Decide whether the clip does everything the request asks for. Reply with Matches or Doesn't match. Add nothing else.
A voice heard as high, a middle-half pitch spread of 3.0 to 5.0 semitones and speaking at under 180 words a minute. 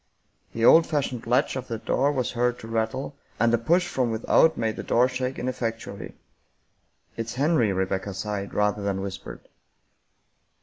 Doesn't match